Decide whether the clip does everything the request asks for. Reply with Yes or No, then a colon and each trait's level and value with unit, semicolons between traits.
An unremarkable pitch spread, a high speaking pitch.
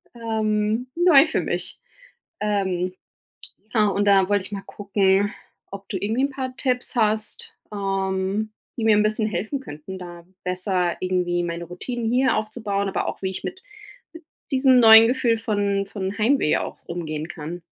Yes: average, 3.1 semitones; high, 205 Hz